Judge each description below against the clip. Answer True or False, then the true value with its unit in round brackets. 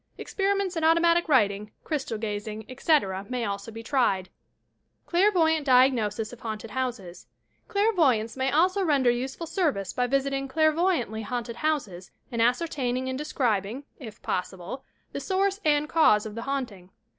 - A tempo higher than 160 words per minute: False (145 wpm)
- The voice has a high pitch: True (255 Hz)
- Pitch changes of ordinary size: False (6.3 semitones)